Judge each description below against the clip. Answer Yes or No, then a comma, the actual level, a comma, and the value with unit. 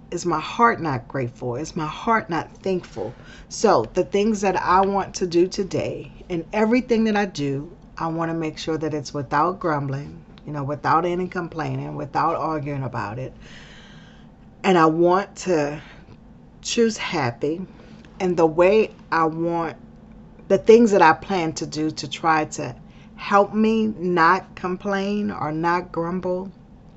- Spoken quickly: No, average, 155 wpm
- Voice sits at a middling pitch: Yes, medium, 170 Hz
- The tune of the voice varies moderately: Yes, average, 3.9 semitones